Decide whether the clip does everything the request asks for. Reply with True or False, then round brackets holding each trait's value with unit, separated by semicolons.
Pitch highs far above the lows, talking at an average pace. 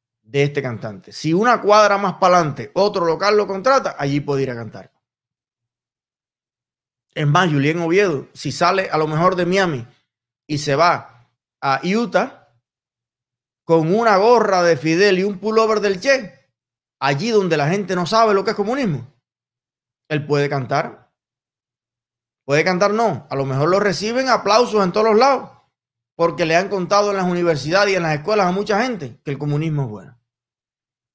True (7.4 semitones; 170 wpm)